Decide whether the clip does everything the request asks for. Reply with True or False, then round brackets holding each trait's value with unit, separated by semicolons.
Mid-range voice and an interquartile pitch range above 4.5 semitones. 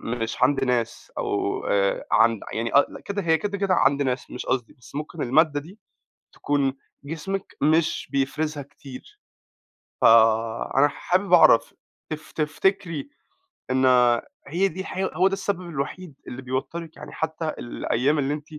True (145 Hz; 4.9 semitones)